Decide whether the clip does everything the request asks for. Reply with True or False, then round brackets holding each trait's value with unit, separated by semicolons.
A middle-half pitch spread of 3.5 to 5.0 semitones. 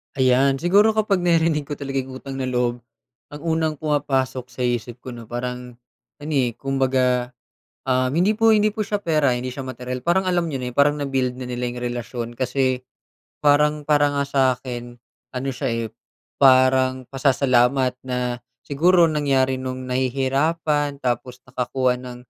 False (2.8 semitones)